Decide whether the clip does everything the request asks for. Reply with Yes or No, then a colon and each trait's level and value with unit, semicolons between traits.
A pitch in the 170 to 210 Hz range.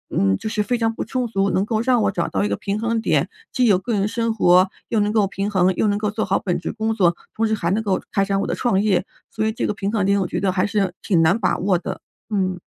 Yes: high, 200 Hz